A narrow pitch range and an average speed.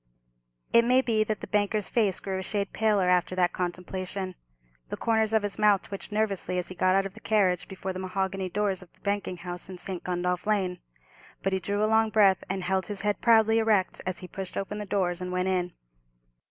No: narrow, 2.3 semitones; fast, 220 wpm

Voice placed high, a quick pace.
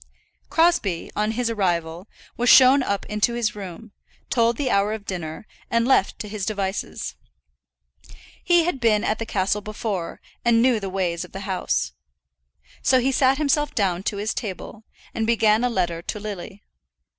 No: high, 215 Hz; average, 170 wpm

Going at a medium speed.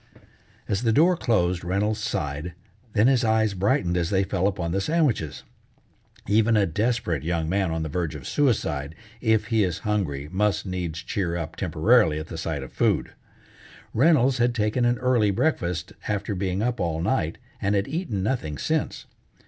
Yes: average, 175 wpm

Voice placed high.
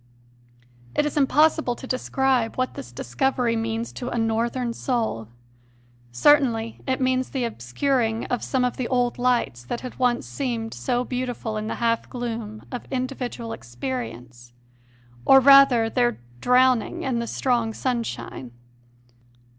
Yes: high, 240 Hz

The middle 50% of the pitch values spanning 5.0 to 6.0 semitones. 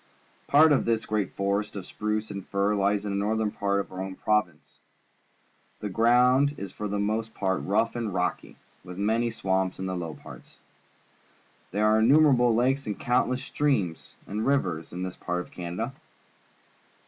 No: average, 3.4 semitones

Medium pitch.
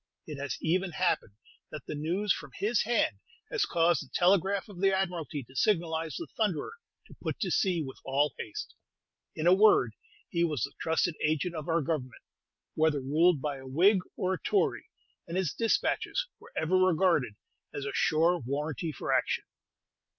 Yes: medium, 165 Hz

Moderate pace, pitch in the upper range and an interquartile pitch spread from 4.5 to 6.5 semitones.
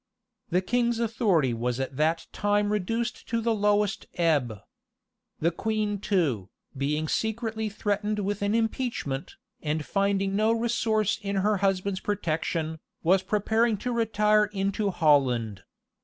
No: slow, 130 wpm; high, 200 Hz; average, 5.1 semitones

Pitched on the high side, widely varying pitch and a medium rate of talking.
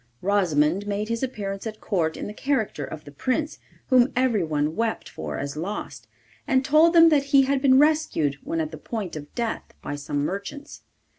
Yes: high, 210 Hz; wide, 9.0 semitones; average, 190 wpm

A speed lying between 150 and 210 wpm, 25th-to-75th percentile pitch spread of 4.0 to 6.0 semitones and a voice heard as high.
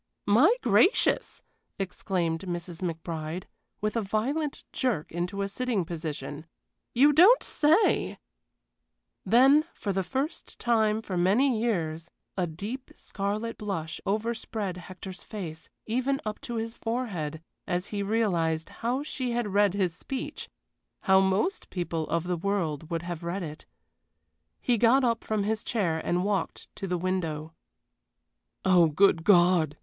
No: average, 140 wpm; average, 5.1 semitones; high, 195 Hz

